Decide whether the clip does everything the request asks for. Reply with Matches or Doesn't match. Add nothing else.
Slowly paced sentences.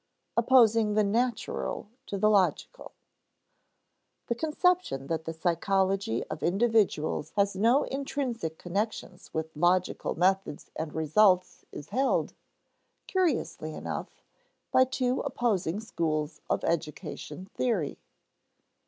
Matches